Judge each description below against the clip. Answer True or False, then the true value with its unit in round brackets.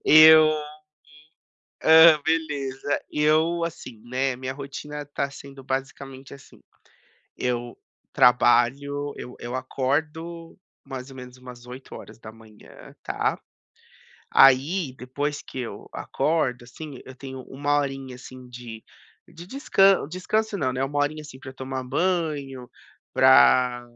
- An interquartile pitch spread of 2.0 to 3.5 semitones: True (3.2 semitones)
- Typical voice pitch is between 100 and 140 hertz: True (135 Hz)